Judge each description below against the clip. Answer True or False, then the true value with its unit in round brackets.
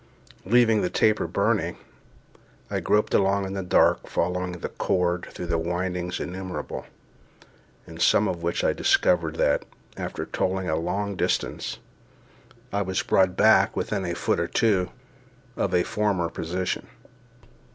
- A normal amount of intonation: False (2.0 semitones)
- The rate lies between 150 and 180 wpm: False (140 wpm)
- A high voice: False (90 Hz)